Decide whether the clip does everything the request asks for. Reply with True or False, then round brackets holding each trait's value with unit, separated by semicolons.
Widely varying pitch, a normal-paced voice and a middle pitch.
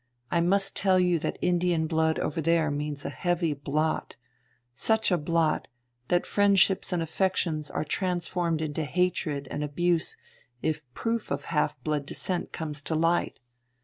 False (2.7 semitones; 150 wpm; 165 Hz)